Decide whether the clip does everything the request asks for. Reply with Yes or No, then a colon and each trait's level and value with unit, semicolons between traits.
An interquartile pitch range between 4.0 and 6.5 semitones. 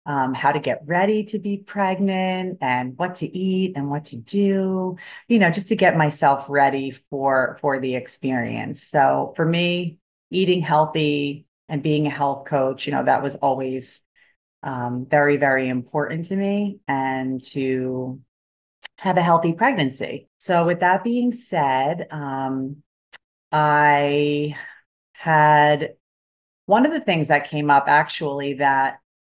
Yes: average, 5.0 semitones